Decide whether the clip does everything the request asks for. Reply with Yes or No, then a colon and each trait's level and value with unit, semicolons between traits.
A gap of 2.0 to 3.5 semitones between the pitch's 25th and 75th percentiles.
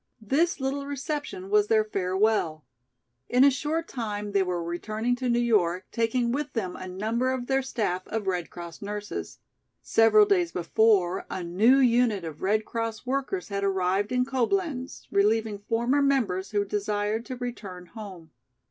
No: average, 4.7 semitones